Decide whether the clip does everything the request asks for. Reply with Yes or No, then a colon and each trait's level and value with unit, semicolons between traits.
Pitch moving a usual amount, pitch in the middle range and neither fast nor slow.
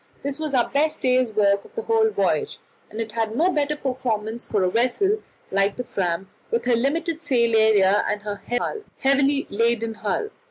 No: average, 5.0 semitones; high, 235 Hz; average, 185 wpm